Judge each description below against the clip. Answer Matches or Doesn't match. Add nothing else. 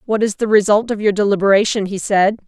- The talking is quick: Matches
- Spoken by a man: Doesn't match